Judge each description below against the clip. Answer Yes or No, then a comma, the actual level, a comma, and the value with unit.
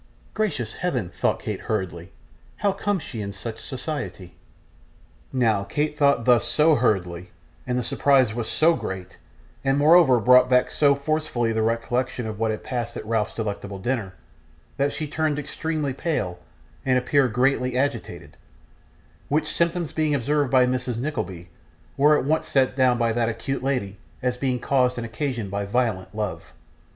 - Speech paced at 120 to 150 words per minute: No, average, 160 wpm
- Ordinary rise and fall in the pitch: Yes, average, 4.4 semitones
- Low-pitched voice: Yes, low, 125 Hz